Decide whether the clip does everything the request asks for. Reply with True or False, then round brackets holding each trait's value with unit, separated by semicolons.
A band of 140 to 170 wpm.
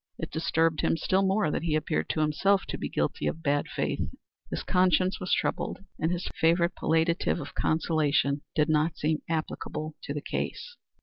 False (180 wpm)